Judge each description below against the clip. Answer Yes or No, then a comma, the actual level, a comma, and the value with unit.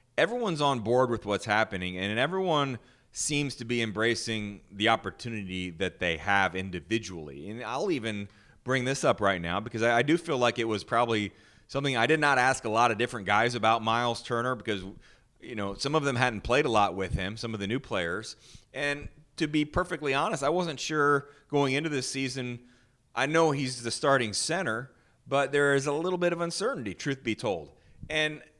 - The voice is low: Yes, low, 120 Hz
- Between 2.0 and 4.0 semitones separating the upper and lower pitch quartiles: No, average, 4.7 semitones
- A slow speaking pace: No, average, 195 wpm